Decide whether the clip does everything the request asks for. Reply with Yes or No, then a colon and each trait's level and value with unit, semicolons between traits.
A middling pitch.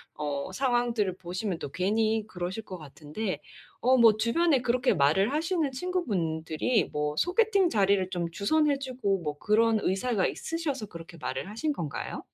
No: high, 215 Hz